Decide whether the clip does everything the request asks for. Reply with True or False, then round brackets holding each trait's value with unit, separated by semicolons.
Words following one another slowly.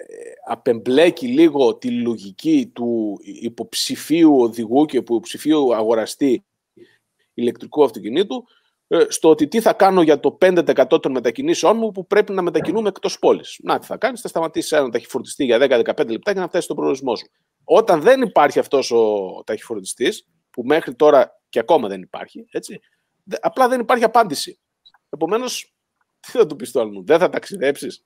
False (150 wpm)